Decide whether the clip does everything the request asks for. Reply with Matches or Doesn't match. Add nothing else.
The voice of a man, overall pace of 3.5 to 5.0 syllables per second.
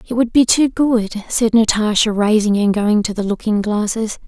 Doesn't match